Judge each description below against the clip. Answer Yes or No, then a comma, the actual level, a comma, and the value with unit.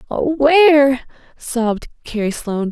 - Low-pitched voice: No, very high, 260 Hz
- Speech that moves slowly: Yes, slow, 90 wpm